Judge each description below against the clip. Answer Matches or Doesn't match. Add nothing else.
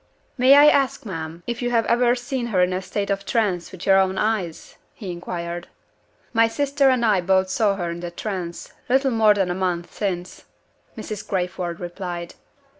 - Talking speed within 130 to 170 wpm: Doesn't match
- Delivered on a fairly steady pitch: Doesn't match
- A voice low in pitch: Doesn't match